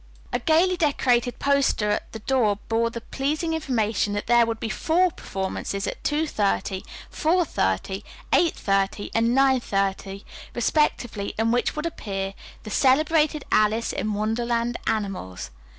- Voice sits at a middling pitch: No, high, 230 Hz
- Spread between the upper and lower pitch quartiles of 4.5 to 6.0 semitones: Yes, wide, 5.5 semitones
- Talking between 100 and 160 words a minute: Yes, average, 145 wpm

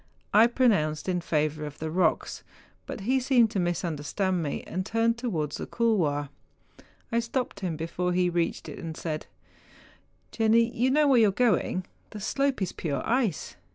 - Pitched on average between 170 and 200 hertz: Yes, high, 190 Hz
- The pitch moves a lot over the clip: Yes, wide, 6.3 semitones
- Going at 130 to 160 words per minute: No, average, 190 wpm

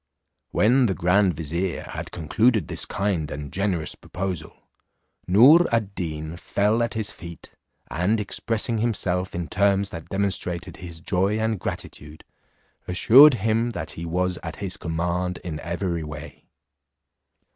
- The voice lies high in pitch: No, very low, 90 Hz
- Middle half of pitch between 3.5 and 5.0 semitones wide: Yes, average, 3.9 semitones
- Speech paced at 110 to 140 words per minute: Yes, slow, 135 wpm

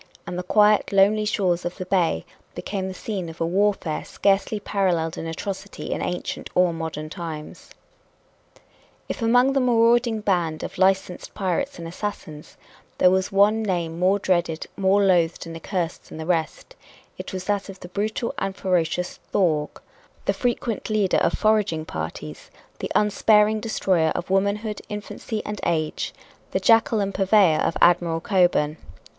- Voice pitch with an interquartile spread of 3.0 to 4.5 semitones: Yes, average, 3.7 semitones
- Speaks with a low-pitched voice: No, high, 190 Hz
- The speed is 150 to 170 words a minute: Yes, average, 155 wpm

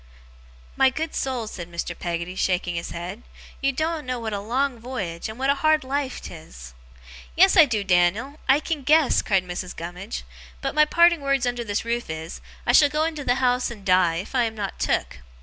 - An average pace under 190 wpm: No, fast, 205 wpm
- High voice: Yes, high, 240 Hz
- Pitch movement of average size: No, wide, 7.3 semitones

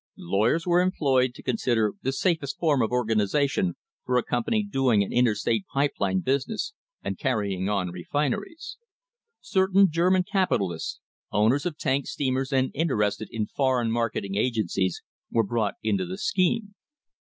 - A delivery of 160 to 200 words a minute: No, average, 150 wpm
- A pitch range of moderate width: No, wide, 7.6 semitones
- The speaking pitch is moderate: No, low, 130 Hz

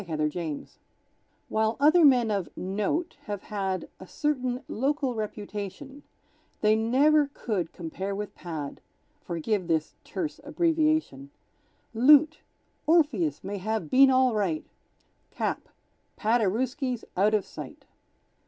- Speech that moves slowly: Yes, slow, 110 wpm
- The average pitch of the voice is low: No, high, 220 Hz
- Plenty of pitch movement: Yes, wide, 6.8 semitones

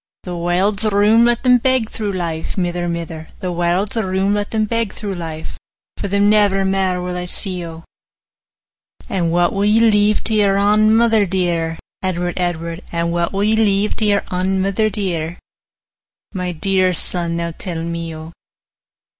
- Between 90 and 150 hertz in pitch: No, high, 190 Hz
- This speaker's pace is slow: No, average, 180 wpm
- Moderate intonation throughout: Yes, average, 3.2 semitones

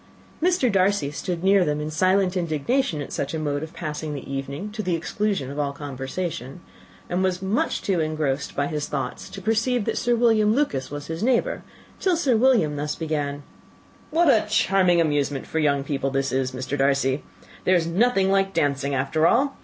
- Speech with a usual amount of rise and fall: No, wide, 6.0 semitones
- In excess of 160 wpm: Yes, average, 190 wpm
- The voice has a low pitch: No, medium, 160 Hz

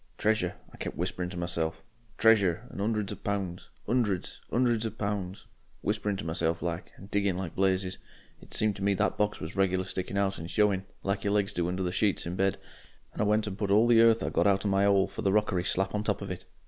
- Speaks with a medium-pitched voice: No, low, 100 Hz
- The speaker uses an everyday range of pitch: No, narrow, 2.3 semitones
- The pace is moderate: No, fast, 235 wpm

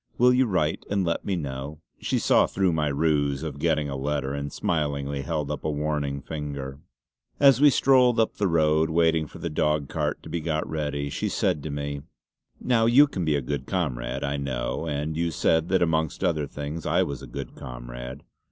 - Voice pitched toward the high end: No, very low, 75 Hz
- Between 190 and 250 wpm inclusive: Yes, fast, 205 wpm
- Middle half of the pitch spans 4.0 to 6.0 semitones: No, average, 2.9 semitones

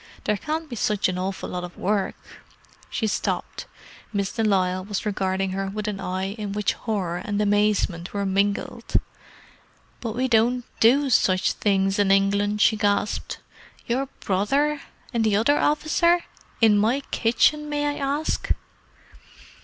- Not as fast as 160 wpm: Yes, average, 150 wpm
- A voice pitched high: Yes, high, 210 Hz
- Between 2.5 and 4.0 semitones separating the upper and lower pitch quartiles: Yes, average, 3.7 semitones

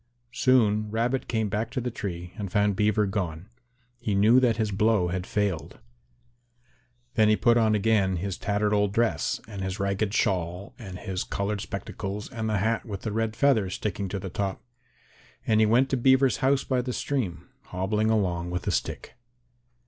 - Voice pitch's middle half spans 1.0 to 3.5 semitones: Yes, average, 2.7 semitones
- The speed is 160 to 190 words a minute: Yes, average, 180 wpm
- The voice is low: Yes, low, 105 Hz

